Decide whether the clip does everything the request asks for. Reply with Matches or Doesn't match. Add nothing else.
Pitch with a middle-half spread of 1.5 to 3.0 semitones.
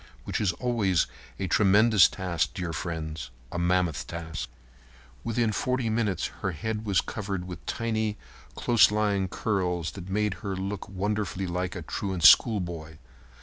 Doesn't match